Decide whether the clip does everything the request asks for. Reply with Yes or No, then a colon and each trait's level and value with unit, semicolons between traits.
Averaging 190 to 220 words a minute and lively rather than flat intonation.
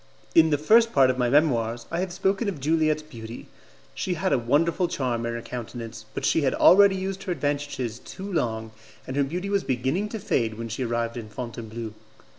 Yes: fast, 205 wpm; wide, 7.0 semitones